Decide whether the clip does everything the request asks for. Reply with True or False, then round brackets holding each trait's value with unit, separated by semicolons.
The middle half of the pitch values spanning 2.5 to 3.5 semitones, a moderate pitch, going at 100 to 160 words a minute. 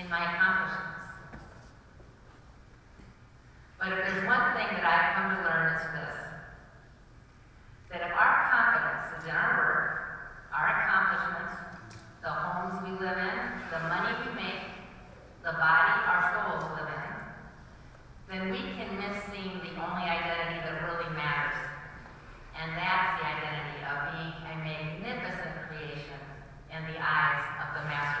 False (3.9 semitones; 165 Hz; 140 wpm)